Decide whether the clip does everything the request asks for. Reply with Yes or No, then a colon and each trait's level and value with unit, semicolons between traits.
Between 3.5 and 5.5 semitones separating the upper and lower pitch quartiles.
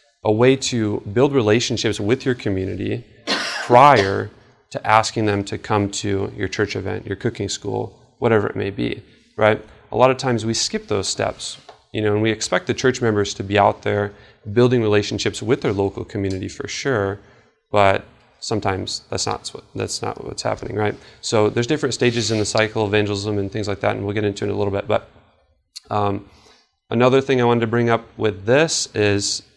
No: average, 2.8 semitones